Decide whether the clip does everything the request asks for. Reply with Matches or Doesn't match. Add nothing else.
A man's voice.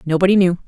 Doesn't match